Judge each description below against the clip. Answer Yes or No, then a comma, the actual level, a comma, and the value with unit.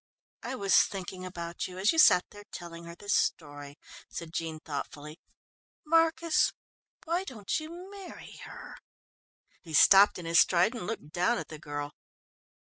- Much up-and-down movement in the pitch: Yes, wide, 6.6 semitones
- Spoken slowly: No, average, 155 wpm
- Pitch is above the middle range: No, medium, 180 Hz